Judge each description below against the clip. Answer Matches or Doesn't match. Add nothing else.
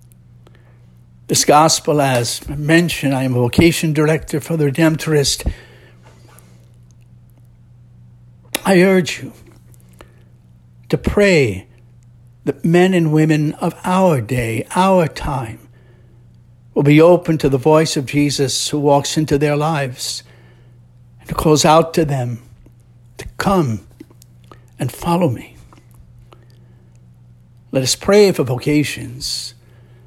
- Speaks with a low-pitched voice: Matches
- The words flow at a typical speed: Doesn't match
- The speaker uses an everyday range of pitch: Matches